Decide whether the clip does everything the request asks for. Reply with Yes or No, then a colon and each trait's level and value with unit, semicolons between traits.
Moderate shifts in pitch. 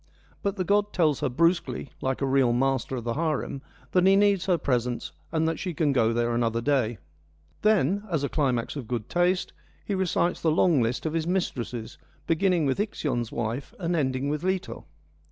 No: wide, 6.2 semitones